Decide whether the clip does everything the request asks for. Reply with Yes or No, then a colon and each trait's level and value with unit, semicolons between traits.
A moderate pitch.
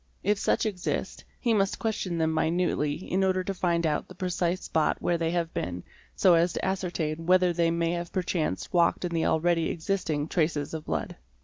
Yes: medium, 170 Hz